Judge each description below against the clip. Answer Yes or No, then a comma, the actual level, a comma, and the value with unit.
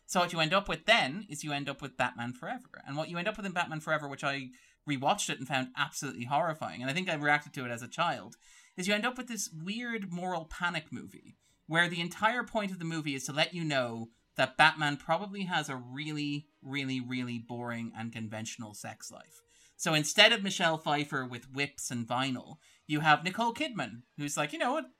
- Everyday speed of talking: No, fast, 225 wpm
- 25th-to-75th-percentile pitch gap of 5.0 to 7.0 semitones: Yes, average, 5.3 semitones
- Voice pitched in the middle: Yes, medium, 150 Hz